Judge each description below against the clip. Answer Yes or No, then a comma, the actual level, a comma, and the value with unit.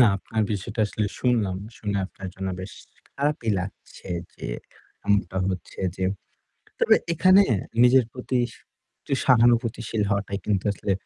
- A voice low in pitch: Yes, low, 110 Hz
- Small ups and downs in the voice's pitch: No, average, 3.8 semitones